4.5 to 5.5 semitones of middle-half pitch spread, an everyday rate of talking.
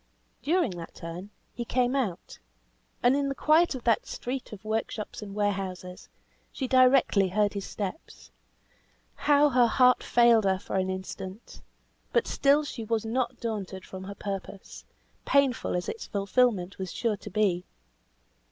Yes: average, 4.9 semitones; average, 150 wpm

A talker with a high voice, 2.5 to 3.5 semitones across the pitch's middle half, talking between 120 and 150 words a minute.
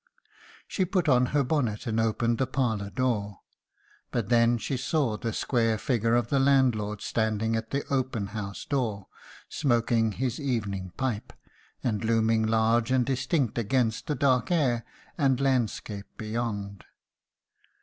No: low, 115 Hz; average, 3.1 semitones; average, 140 wpm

